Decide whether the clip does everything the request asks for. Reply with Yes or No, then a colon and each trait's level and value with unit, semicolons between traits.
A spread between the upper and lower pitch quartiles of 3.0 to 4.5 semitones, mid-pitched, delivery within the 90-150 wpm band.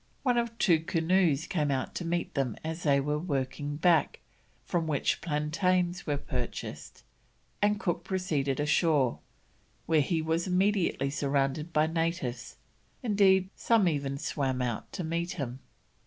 Yes: average, 4.2 semitones; medium, 160 Hz; average, 140 wpm